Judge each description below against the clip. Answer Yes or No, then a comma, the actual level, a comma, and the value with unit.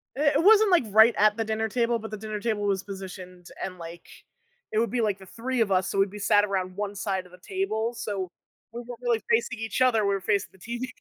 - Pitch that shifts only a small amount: No, average, 3.3 semitones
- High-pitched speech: Yes, high, 215 Hz